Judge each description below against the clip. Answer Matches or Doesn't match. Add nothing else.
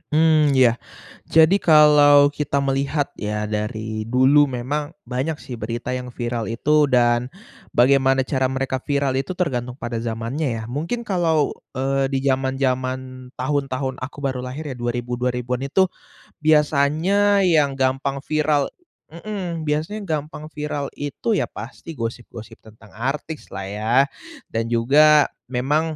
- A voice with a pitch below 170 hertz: Matches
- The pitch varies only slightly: Doesn't match